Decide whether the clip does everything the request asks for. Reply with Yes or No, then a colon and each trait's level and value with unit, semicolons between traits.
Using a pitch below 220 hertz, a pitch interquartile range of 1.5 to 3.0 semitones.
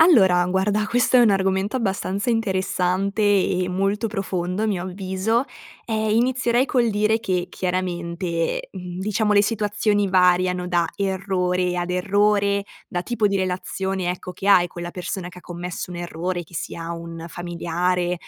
Yes: high, 190 Hz; narrow, 2.5 semitones